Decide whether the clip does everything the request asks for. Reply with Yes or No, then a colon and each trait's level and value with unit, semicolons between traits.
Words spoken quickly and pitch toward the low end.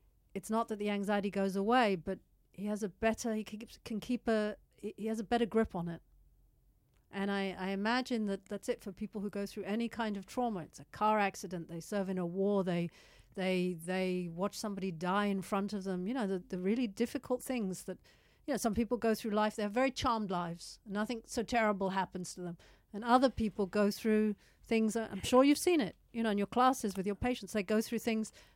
No: fast, 225 wpm; high, 210 Hz